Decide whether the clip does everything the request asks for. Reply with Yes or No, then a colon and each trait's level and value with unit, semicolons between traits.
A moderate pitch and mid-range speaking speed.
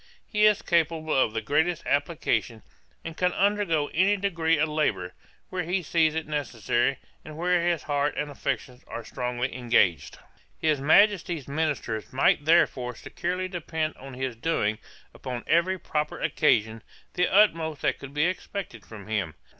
Yes: medium, 155 Hz; average, 155 wpm